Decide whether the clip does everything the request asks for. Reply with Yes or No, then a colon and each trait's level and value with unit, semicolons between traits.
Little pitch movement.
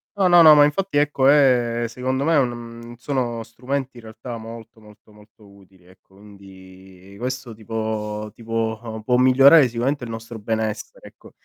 No: average, 3.5 semitones